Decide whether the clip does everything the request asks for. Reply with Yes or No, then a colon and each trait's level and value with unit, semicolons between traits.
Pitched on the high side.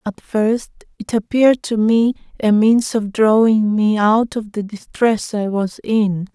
Yes: high, 215 Hz